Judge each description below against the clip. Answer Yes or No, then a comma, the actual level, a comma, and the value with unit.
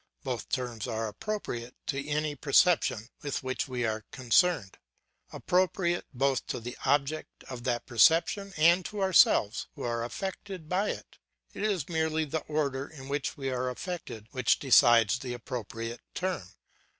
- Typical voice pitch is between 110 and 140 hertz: Yes, low, 135 Hz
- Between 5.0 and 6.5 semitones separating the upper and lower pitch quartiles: Yes, average, 5.3 semitones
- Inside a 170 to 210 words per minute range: No, average, 150 wpm